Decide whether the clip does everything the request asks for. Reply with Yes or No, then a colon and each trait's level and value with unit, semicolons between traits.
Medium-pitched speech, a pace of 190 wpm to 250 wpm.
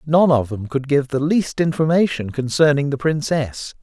No: medium, 145 Hz; average, 170 wpm